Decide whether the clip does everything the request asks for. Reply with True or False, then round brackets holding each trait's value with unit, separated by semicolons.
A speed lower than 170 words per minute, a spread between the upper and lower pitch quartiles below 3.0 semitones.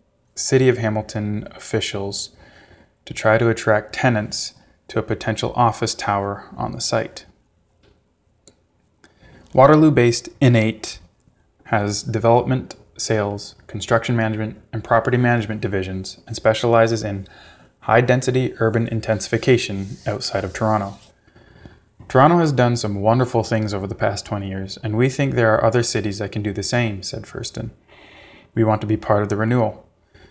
True (145 wpm; 2.6 semitones)